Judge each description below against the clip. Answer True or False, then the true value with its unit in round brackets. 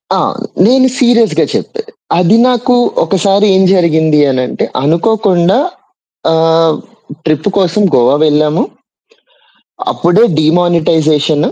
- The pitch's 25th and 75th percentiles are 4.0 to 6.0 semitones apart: True (5.1 semitones)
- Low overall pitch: False (170 Hz)